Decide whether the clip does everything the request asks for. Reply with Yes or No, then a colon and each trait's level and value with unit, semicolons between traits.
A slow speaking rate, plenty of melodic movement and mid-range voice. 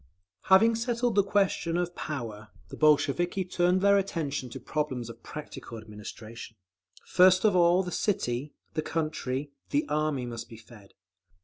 No: average, 145 wpm; wide, 7.3 semitones; medium, 155 Hz